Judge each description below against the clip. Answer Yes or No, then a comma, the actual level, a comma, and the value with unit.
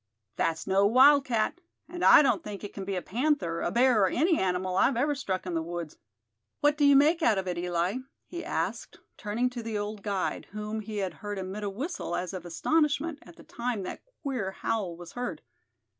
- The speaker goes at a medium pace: No, fast, 210 wpm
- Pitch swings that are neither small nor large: No, wide, 6.3 semitones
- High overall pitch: Yes, high, 210 Hz